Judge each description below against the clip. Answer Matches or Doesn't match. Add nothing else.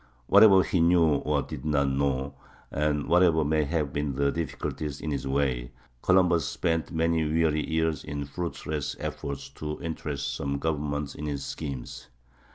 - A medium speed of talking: Matches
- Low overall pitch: Matches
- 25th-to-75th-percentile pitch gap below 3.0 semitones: Matches